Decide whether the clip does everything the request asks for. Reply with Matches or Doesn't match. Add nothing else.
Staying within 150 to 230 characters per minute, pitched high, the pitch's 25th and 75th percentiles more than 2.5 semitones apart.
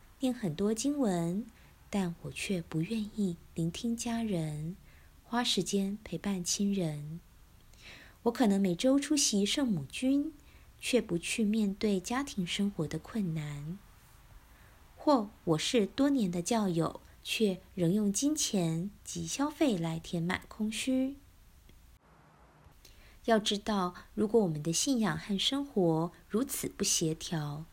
Matches